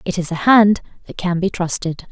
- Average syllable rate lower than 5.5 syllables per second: Yes, 5.2 syllables/s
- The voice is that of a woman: Yes, female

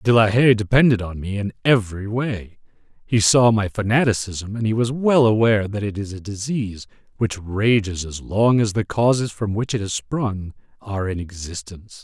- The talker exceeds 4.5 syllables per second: Yes, 5.1 syllables/s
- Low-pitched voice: Yes, low, 105 Hz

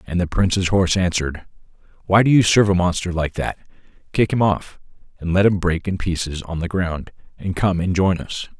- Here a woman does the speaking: No, male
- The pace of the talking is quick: Yes, fast, 210 wpm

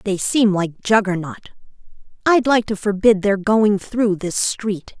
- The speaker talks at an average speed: Yes, average, 155 wpm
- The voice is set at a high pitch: Yes, high, 205 Hz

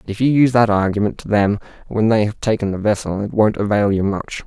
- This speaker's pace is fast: Yes, fast, 255 wpm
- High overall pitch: No, low, 105 Hz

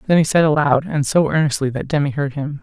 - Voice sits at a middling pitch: Yes, medium, 145 Hz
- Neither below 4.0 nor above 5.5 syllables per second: No, 6.2 syllables/s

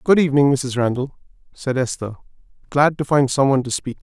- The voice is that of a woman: No, male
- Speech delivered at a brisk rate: No, average, 190 wpm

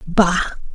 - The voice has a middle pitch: Yes, medium, 180 Hz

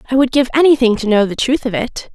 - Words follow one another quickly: Yes, fast, 280 wpm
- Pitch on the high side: Yes, high, 245 Hz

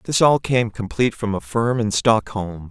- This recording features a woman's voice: No, male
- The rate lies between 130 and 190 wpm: No, average, 200 wpm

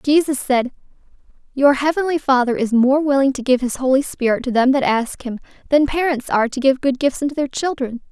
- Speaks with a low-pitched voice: No, very high, 265 Hz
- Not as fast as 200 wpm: No, fast, 205 wpm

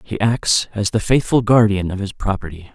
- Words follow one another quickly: No, average, 195 wpm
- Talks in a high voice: No, low, 105 Hz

